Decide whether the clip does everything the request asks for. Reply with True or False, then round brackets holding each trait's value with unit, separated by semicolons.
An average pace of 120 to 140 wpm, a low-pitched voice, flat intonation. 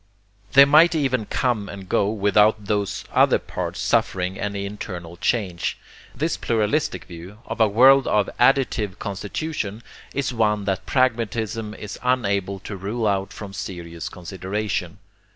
False (135 wpm; 105 Hz; 3.2 semitones)